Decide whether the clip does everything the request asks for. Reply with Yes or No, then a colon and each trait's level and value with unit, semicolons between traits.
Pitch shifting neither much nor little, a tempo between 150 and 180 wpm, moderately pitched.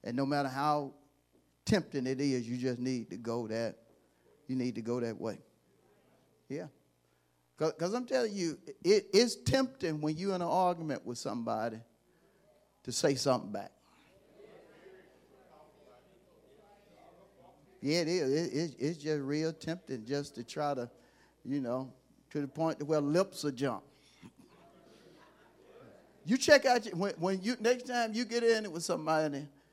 No: wide, 6.5 semitones; average, 155 wpm; medium, 150 Hz